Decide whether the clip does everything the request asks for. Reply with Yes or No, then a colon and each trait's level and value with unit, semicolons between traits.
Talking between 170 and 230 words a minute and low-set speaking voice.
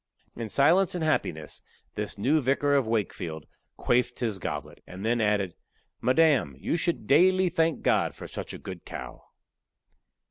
No: average, 150 wpm; low, 125 Hz